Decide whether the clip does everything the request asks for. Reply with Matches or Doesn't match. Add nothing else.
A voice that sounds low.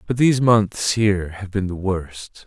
Matches